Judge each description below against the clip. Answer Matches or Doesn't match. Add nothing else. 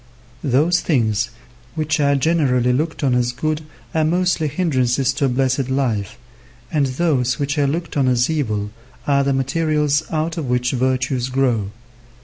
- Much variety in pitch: Doesn't match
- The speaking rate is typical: Matches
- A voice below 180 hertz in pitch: Matches